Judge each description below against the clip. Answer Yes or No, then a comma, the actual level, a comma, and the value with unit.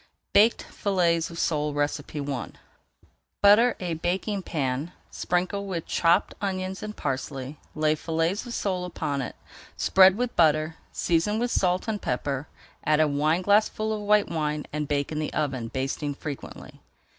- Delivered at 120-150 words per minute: Yes, average, 145 wpm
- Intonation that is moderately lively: Yes, average, 4.7 semitones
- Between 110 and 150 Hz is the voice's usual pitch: No, medium, 165 Hz